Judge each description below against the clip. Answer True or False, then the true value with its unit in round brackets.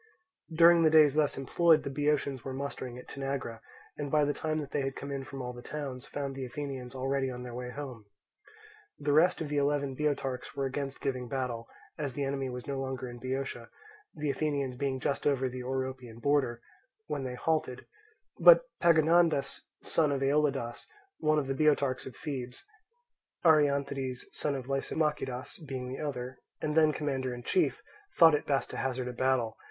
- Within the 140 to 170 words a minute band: False (185 wpm)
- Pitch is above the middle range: False (135 Hz)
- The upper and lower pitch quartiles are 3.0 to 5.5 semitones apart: False (2.4 semitones)